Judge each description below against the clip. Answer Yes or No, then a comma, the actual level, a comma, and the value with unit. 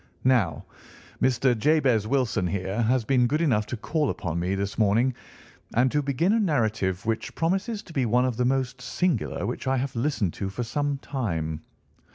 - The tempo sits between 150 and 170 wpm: No, average, 185 wpm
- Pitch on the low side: Yes, low, 125 Hz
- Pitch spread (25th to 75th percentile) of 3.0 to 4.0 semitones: No, average, 4.8 semitones